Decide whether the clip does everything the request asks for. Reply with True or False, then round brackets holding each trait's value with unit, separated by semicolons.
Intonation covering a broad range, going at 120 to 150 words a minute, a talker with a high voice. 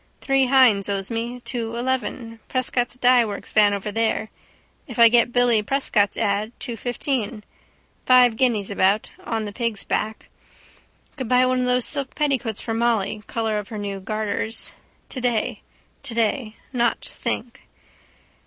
False (2.8 semitones; 145 wpm; 230 Hz)